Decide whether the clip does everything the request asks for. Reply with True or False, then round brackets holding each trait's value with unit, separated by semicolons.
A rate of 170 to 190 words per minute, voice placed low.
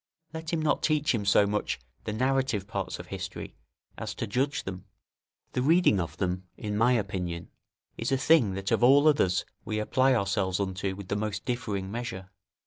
True (185 wpm; 105 Hz)